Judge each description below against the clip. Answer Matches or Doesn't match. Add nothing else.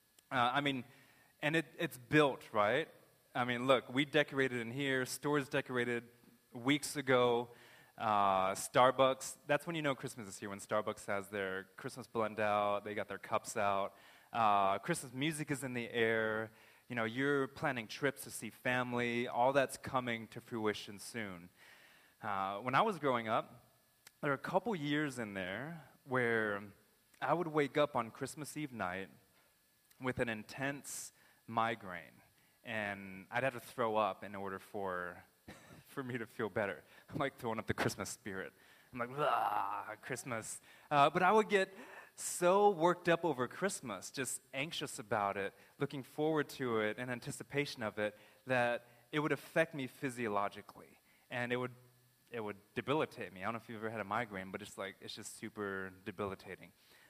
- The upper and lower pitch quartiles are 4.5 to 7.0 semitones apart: Matches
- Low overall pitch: Matches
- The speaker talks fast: Doesn't match